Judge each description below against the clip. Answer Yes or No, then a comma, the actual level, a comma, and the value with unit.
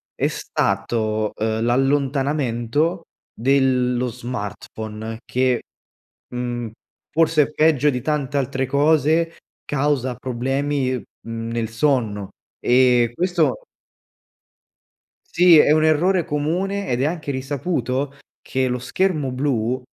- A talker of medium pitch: No, low, 130 Hz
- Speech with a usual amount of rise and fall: Yes, average, 3.7 semitones